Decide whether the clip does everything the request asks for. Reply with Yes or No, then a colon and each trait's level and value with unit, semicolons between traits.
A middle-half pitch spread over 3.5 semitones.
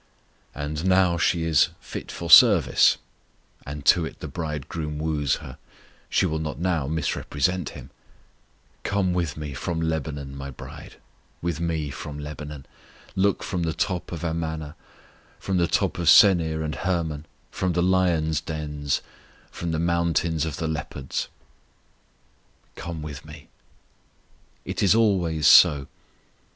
No: narrow, 2.5 semitones